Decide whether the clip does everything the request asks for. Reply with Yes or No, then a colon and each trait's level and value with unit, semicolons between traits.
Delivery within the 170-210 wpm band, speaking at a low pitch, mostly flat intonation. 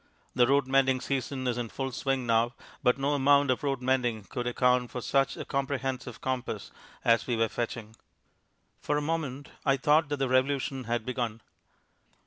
Yes: average, 175 wpm; low, 130 Hz; narrow, 2.1 semitones